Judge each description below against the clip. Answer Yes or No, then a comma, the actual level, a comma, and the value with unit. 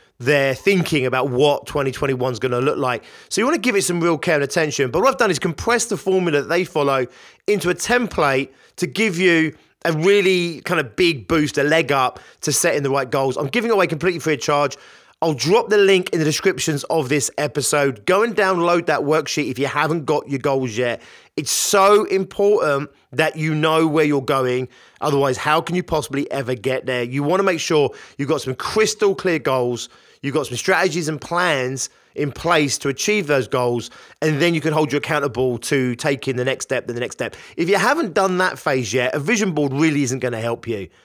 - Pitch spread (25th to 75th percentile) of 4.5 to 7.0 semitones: Yes, average, 4.8 semitones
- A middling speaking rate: No, fast, 225 wpm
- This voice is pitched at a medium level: Yes, medium, 155 Hz